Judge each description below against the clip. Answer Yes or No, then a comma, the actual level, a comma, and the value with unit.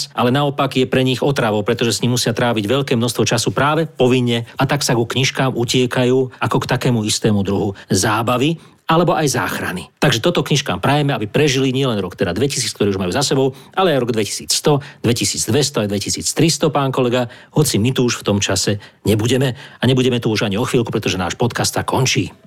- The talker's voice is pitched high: No, low, 125 Hz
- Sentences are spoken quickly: Yes, fast, 200 wpm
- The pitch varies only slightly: No, average, 3.7 semitones